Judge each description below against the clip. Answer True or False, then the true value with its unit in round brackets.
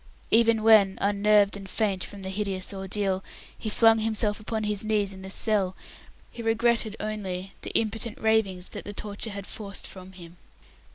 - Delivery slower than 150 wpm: False (170 wpm)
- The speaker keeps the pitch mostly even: True (2.2 semitones)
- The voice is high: True (205 Hz)